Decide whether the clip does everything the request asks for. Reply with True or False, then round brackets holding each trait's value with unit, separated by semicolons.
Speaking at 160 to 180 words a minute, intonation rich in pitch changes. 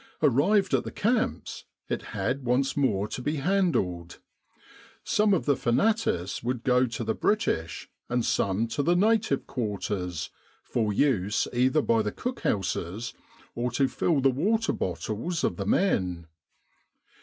False (145 wpm; 8.2 semitones)